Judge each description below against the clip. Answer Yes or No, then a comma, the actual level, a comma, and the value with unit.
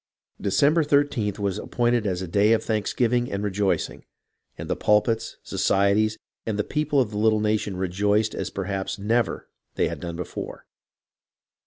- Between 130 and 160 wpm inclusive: Yes, average, 155 wpm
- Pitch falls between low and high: No, low, 105 Hz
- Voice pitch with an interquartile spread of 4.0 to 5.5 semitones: No, narrow, 2.5 semitones